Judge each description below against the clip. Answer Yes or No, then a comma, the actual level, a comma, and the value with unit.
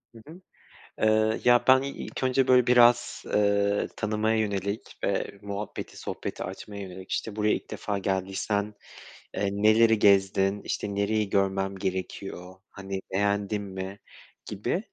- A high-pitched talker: No, low, 100 Hz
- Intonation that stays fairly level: Yes, narrow, 2.0 semitones